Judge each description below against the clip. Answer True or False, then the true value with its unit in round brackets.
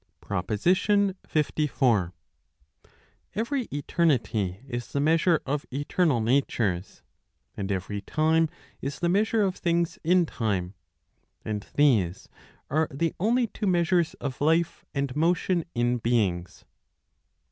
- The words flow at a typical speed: False (115 wpm)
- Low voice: False (145 Hz)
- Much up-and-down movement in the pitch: True (7.5 semitones)